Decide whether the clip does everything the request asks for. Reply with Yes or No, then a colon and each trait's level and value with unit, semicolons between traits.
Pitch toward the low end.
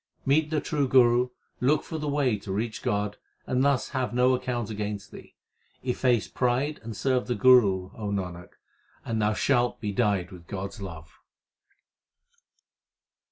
Yes: low, 120 Hz